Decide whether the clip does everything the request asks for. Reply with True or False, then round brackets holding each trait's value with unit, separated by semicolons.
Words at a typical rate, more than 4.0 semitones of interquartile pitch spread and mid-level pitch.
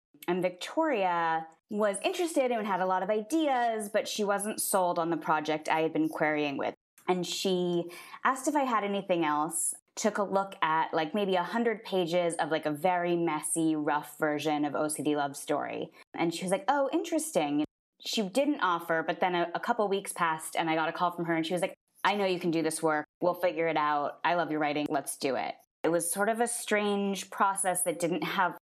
False (220 wpm; 4.6 semitones; 180 Hz)